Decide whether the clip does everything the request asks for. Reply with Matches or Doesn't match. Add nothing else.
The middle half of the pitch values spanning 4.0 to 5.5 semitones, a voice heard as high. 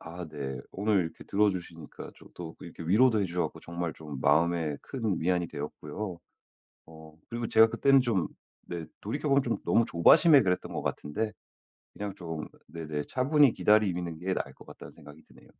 Doesn't match